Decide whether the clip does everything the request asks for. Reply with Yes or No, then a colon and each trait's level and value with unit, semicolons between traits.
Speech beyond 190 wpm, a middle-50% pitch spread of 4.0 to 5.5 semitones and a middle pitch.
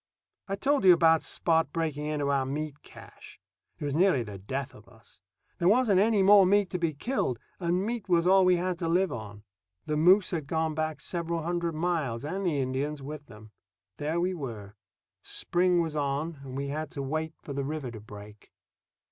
Yes: average, 200 wpm; average, 4.4 semitones; medium, 155 Hz